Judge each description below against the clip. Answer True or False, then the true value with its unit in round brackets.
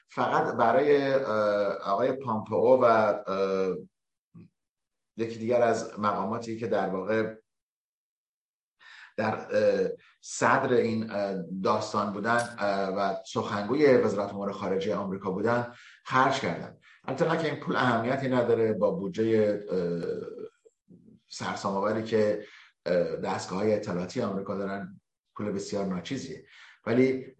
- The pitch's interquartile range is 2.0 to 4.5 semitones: True (3.6 semitones)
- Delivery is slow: True (95 wpm)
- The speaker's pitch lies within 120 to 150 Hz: False (110 Hz)